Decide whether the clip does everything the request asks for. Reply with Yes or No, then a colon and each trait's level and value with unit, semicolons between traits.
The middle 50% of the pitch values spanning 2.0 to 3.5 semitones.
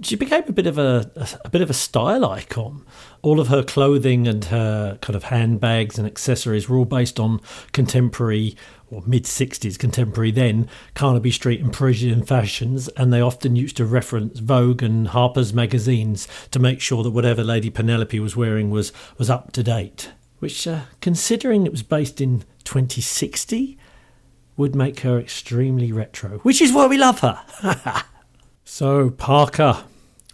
Yes: average, 3.0 semitones